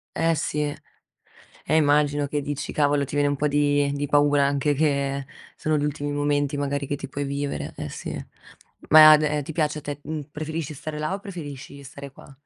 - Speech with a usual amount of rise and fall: No, narrow, 1.1 semitones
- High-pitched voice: No, medium, 145 Hz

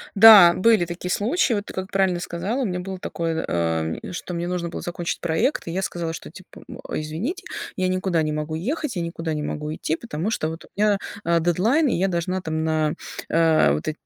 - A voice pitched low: No, medium, 175 Hz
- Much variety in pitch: No, average, 3.2 semitones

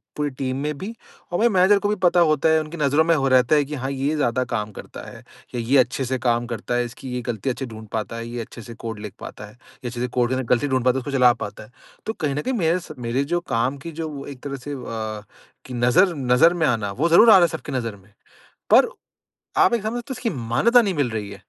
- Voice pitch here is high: No, low, 130 Hz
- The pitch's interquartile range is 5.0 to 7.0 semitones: Yes, average, 5.3 semitones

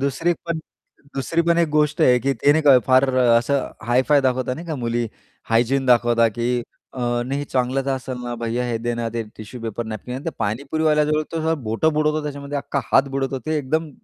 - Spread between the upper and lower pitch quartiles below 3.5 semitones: No, average, 4.0 semitones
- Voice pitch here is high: No, low, 135 Hz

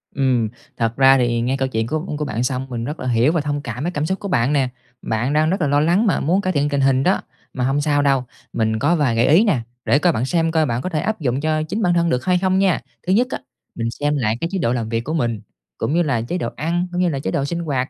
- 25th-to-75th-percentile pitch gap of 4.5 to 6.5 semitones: Yes, average, 5.1 semitones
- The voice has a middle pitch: Yes, medium, 145 Hz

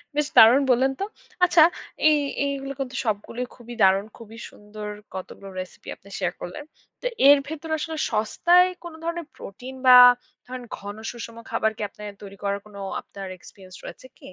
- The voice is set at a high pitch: Yes, high, 235 Hz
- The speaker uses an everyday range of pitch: No, wide, 5.8 semitones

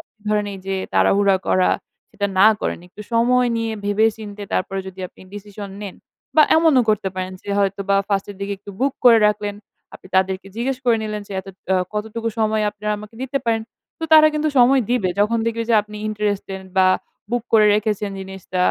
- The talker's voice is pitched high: Yes, high, 210 Hz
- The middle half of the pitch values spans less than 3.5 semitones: Yes, narrow, 2.6 semitones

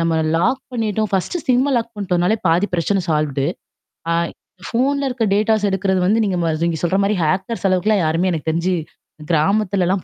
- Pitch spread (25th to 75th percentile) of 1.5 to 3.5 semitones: No, average, 4.2 semitones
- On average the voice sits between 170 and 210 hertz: Yes, high, 190 Hz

